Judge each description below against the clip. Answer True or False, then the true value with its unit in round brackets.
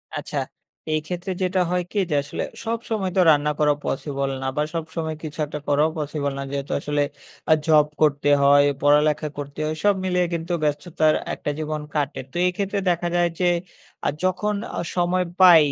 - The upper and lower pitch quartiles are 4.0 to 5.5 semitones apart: False (3.5 semitones)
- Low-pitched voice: False (155 Hz)